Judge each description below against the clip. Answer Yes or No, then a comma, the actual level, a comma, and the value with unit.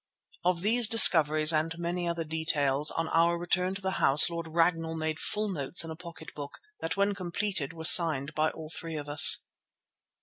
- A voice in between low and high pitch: Yes, medium, 165 Hz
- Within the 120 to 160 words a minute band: No, average, 190 wpm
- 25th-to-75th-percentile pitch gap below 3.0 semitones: Yes, narrow, 2.4 semitones